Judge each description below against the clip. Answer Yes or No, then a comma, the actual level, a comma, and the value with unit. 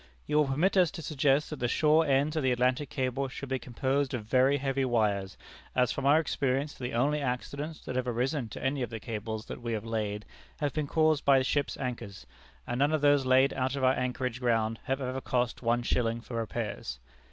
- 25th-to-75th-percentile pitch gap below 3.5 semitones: Yes, average, 2.9 semitones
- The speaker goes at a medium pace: No, fast, 215 wpm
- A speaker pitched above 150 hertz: No, low, 130 Hz